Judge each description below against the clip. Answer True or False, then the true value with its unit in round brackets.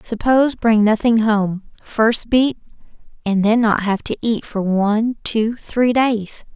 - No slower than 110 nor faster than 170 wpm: True (155 wpm)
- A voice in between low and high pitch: False (220 Hz)